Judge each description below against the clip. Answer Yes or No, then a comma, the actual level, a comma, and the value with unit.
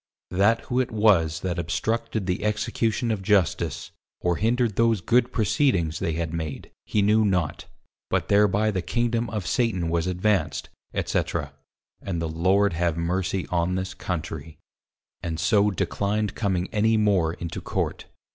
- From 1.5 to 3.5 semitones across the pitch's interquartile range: No, average, 4.2 semitones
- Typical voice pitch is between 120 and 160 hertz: No, very low, 95 Hz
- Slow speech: No, average, 150 wpm